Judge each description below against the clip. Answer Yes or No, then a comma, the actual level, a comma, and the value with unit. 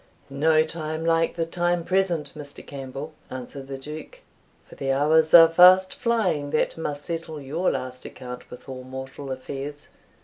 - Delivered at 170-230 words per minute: No, average, 160 wpm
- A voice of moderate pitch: Yes, medium, 155 Hz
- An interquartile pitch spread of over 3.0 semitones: Yes, average, 3.4 semitones